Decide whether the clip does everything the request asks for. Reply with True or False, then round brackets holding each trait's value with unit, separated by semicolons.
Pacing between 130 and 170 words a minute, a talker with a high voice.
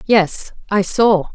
True (135 wpm; 195 Hz)